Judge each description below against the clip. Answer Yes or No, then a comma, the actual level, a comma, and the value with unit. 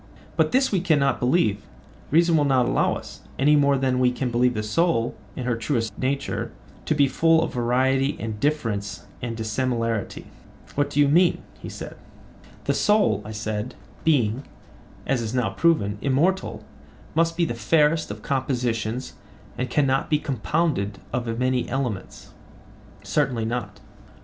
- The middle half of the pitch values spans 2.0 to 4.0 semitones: No, average, 4.5 semitones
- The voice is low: Yes, low, 130 Hz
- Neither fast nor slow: Yes, average, 150 wpm